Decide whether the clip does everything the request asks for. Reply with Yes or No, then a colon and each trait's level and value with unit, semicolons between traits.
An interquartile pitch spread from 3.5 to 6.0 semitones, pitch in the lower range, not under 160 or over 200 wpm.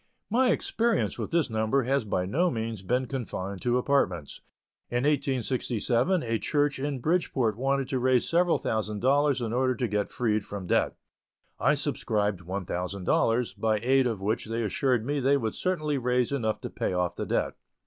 Yes: average, 4.4 semitones; low, 125 Hz; average, 180 wpm